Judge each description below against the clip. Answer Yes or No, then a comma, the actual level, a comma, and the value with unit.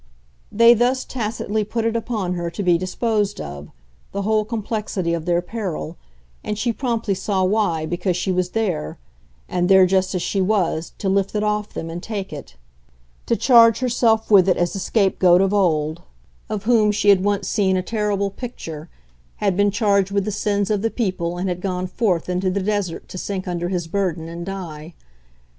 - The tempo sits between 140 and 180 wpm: No, average, 190 wpm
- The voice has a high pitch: Yes, high, 195 Hz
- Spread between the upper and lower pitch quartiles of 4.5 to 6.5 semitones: No, average, 3.1 semitones